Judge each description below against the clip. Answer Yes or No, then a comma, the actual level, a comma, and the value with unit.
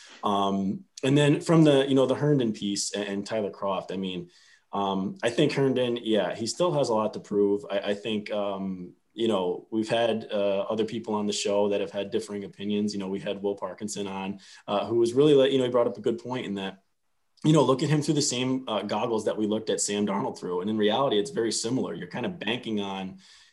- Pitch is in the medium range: No, low, 105 Hz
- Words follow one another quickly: Yes, fast, 245 wpm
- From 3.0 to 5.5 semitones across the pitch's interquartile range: Yes, average, 3.4 semitones